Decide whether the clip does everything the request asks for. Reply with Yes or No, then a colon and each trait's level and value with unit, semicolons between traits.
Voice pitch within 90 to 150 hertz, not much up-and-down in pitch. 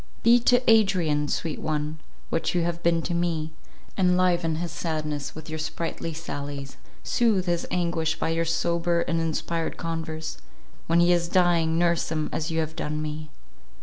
No: medium, 165 Hz; narrow, 1.6 semitones